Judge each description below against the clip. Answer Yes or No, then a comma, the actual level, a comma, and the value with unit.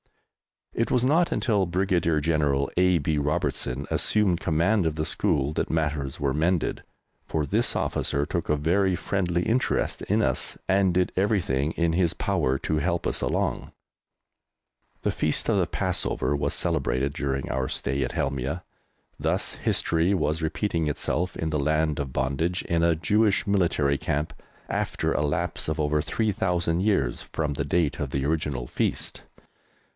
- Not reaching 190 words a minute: Yes, average, 160 wpm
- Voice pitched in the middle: No, very low, 80 Hz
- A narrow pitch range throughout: No, average, 4.0 semitones